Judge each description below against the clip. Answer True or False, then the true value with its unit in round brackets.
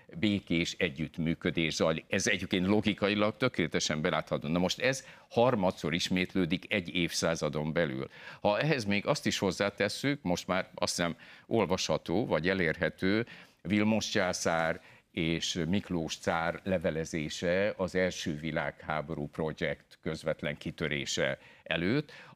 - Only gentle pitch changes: False (3.7 semitones)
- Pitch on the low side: True (90 Hz)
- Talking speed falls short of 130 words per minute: True (115 wpm)